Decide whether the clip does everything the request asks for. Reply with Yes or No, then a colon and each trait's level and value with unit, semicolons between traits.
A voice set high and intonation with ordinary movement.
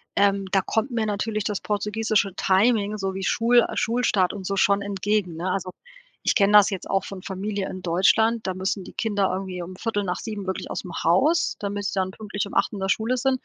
No: high, 200 Hz; narrow, 2.3 semitones